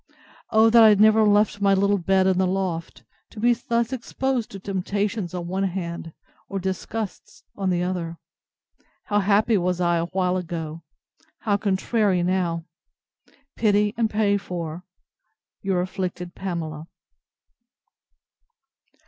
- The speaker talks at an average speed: No, slow, 130 wpm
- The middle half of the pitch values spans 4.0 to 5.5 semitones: No, average, 2.9 semitones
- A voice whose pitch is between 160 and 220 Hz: Yes, high, 190 Hz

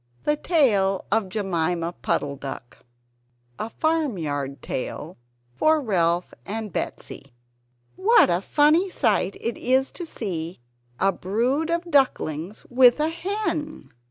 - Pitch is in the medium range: No, high, 220 Hz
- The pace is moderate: No, slow, 120 wpm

